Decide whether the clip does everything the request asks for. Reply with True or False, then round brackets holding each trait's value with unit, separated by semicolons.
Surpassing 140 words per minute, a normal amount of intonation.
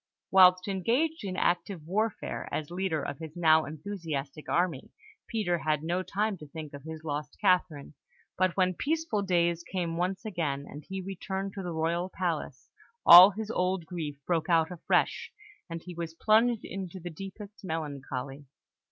True (160 wpm; 3.4 semitones)